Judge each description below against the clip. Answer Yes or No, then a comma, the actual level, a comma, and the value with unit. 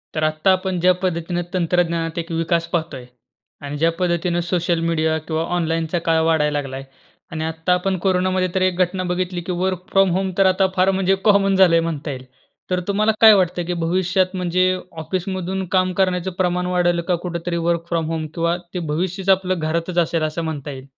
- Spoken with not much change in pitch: Yes, narrow, 2.2 semitones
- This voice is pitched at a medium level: Yes, medium, 175 Hz